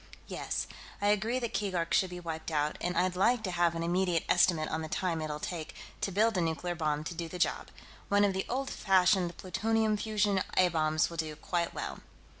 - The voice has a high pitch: No, medium, 180 Hz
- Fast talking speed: Yes, fast, 215 wpm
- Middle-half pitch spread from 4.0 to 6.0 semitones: No, average, 3.6 semitones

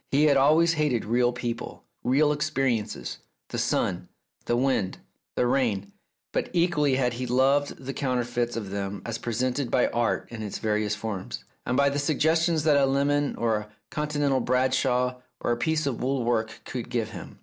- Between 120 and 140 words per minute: No, average, 175 wpm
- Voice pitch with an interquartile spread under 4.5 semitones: Yes, average, 3.4 semitones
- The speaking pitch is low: Yes, low, 125 Hz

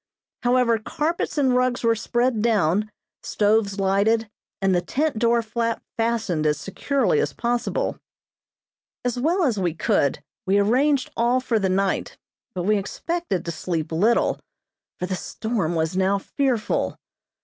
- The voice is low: No, high, 220 Hz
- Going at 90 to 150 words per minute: Yes, average, 145 wpm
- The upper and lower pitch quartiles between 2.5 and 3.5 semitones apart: No, average, 4.4 semitones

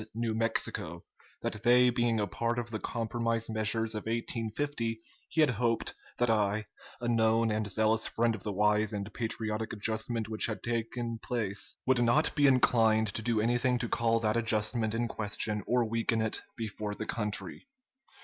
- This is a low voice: Yes, low, 115 Hz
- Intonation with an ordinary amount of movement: No, narrow, 1.5 semitones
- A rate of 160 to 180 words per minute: Yes, average, 175 wpm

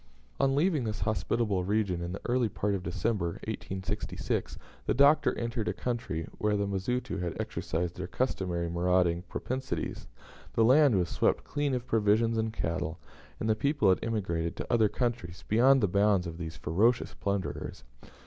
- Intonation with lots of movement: No, average, 5.0 semitones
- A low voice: Yes, low, 105 Hz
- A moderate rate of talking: Yes, average, 165 wpm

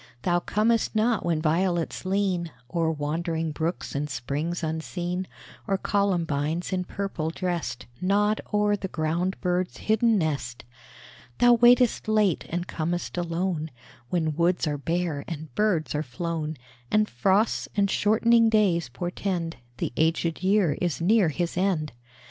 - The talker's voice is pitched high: No, medium, 175 Hz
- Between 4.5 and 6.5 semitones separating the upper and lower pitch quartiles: No, average, 3.8 semitones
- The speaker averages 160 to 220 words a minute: No, slow, 135 wpm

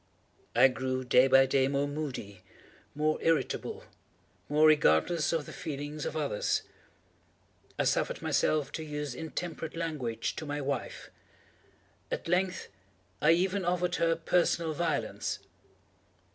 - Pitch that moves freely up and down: No, average, 3.4 semitones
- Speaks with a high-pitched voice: No, medium, 150 Hz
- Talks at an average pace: No, slow, 125 wpm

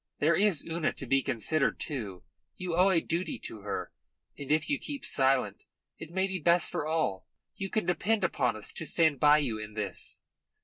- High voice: No, medium, 155 Hz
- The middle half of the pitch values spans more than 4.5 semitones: Yes, average, 5.1 semitones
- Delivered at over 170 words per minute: Yes, average, 195 wpm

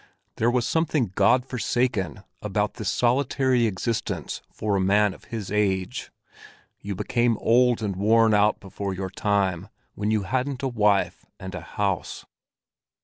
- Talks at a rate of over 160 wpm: No, average, 145 wpm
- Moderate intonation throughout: Yes, average, 3.7 semitones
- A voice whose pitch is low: Yes, low, 105 Hz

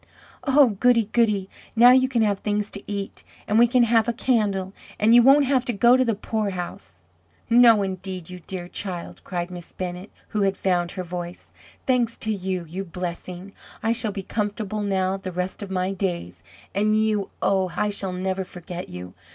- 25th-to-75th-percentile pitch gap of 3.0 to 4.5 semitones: Yes, average, 3.5 semitones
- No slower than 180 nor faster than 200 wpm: Yes, average, 190 wpm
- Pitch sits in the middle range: No, high, 200 Hz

